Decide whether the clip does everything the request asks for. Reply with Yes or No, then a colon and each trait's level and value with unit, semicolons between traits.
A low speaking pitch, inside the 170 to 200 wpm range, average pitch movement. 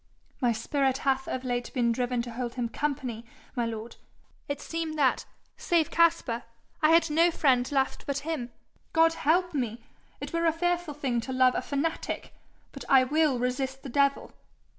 No: very high, 270 Hz; average, 175 wpm; average, 4.3 semitones